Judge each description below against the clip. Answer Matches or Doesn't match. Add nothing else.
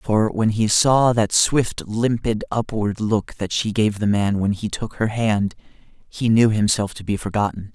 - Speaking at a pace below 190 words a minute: Doesn't match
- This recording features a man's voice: Matches